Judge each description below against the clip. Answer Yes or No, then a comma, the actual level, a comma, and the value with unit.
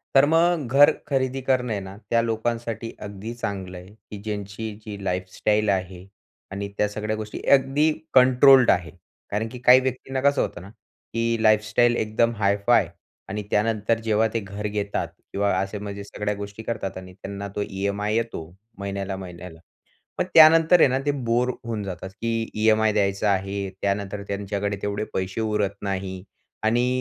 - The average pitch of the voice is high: No, low, 105 Hz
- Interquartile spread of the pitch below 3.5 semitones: Yes, average, 2.8 semitones